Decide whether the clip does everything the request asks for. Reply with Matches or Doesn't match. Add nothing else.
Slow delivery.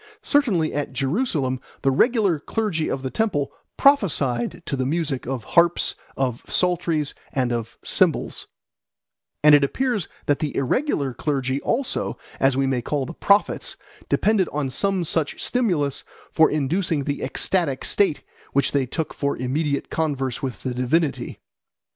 Doesn't match